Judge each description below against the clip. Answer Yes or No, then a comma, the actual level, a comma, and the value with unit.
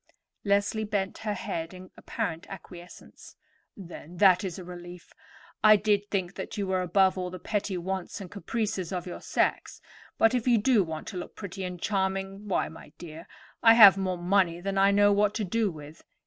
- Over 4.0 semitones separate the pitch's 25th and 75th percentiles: No, narrow, 2.4 semitones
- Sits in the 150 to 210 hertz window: Yes, high, 190 Hz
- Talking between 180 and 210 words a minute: Yes, average, 190 wpm